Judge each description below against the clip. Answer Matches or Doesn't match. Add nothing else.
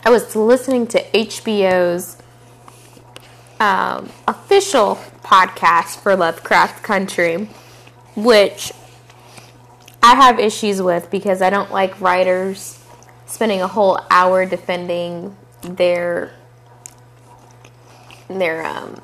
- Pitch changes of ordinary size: Doesn't match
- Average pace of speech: Doesn't match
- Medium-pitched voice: Matches